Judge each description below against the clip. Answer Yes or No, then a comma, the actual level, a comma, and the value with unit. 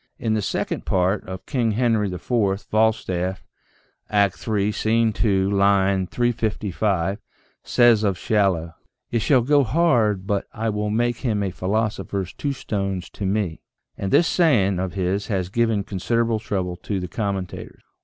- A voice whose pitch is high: No, low, 105 Hz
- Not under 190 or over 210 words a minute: No, average, 155 wpm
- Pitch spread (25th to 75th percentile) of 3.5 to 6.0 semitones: No, average, 3.0 semitones